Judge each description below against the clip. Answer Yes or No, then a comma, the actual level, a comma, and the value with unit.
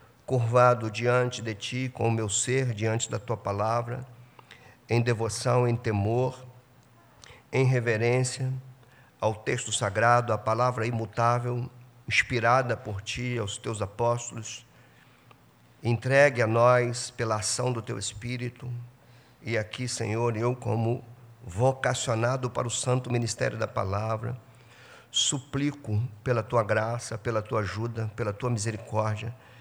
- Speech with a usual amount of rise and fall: No, narrow, 1.7 semitones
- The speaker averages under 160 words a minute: Yes, slow, 120 wpm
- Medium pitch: No, low, 120 Hz